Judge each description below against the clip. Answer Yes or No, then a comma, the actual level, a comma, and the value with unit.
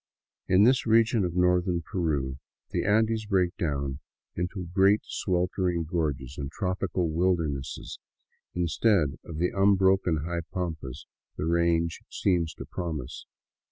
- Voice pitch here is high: No, very low, 85 Hz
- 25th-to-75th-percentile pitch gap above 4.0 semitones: No, average, 3.2 semitones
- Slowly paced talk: Yes, slow, 125 wpm